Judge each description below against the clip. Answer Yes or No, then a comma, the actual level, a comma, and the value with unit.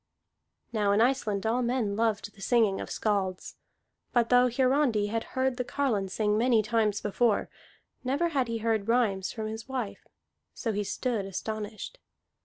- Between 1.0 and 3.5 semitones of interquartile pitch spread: Yes, average, 3.1 semitones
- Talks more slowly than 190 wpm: Yes, average, 160 wpm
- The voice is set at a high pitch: Yes, high, 225 Hz